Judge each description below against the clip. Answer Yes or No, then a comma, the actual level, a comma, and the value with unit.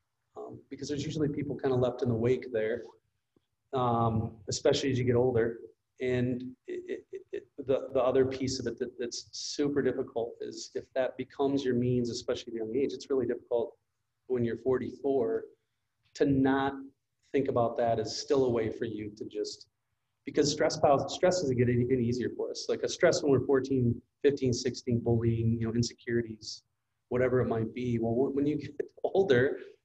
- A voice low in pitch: Yes, low, 130 Hz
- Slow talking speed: No, average, 185 wpm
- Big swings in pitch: No, average, 3.1 semitones